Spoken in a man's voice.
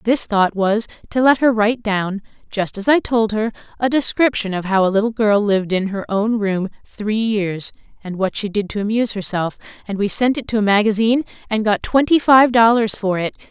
No: female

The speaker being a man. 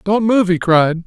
Yes: male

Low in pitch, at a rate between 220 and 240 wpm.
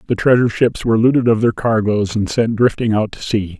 Yes: low, 110 Hz; fast, 235 wpm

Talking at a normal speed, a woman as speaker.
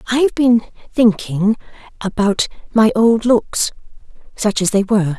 No: slow, 125 wpm; female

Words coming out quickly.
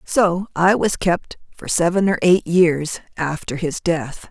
No: average, 165 wpm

